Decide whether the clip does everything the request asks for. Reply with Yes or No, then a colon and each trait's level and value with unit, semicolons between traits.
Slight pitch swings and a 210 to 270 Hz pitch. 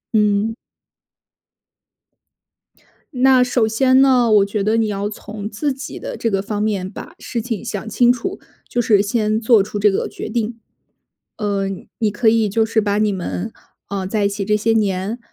Yes: narrow, 2.2 semitones; high, 215 Hz